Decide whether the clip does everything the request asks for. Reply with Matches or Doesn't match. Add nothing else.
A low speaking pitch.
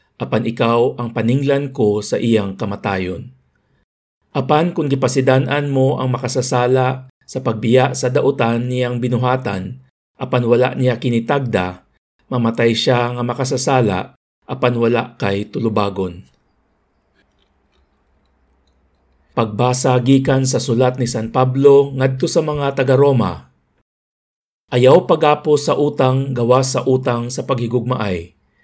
Matches